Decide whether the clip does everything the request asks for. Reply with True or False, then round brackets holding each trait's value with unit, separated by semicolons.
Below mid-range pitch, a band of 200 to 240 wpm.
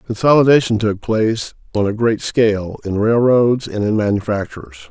False (110 Hz; 145 wpm)